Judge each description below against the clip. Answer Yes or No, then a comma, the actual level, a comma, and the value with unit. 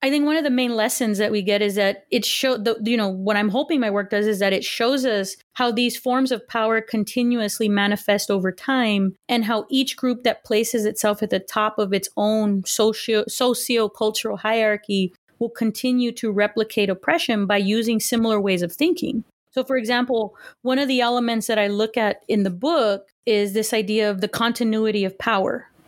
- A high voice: Yes, high, 220 Hz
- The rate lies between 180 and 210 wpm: Yes, average, 200 wpm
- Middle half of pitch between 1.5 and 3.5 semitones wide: Yes, narrow, 2.6 semitones